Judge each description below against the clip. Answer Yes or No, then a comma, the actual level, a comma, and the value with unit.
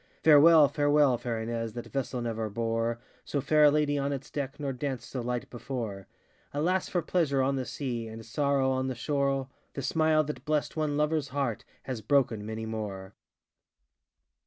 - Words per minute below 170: No, average, 175 wpm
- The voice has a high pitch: No, low, 135 Hz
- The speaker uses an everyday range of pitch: Yes, average, 3.9 semitones